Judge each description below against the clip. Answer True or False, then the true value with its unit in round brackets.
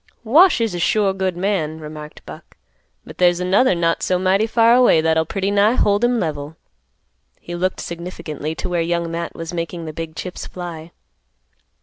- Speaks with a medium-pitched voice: True (175 Hz)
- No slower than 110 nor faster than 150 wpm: False (180 wpm)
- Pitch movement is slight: False (3.5 semitones)